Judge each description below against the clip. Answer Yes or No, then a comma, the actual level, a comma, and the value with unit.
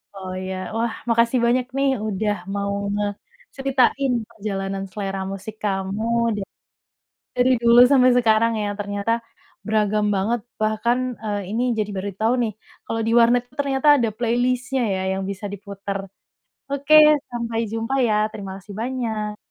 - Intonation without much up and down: No, average, 3.1 semitones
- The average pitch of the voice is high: Yes, high, 220 Hz